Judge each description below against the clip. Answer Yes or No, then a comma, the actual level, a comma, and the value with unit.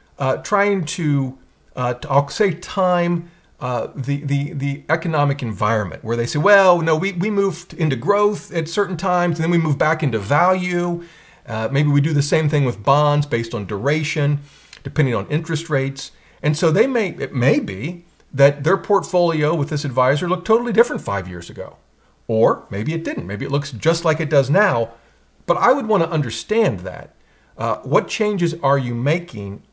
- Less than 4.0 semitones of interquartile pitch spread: No, average, 4.3 semitones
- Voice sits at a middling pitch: Yes, medium, 150 Hz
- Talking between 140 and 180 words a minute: No, average, 190 wpm